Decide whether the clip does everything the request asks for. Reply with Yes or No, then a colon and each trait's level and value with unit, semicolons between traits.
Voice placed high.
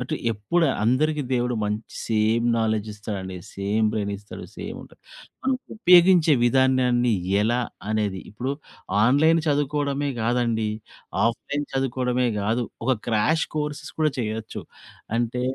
No: low, 125 Hz